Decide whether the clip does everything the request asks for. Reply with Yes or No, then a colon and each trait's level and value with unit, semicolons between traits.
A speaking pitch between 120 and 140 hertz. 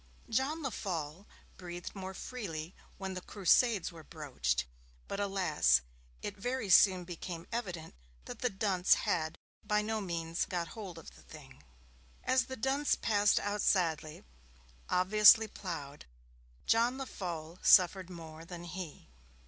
No: medium, 185 Hz